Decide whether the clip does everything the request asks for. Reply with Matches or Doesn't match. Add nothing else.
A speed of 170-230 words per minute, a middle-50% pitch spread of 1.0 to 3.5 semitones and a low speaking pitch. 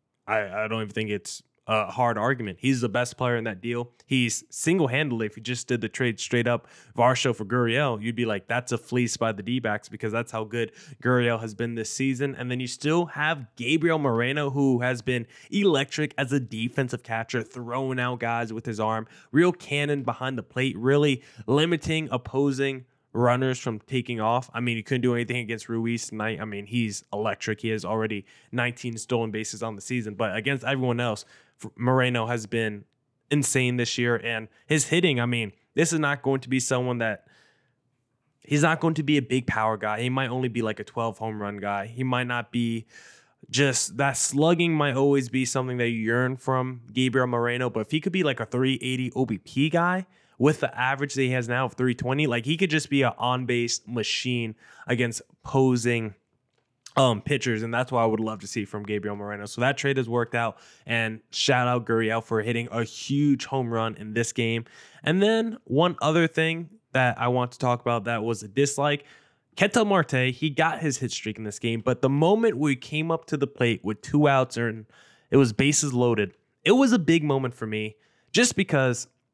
Matches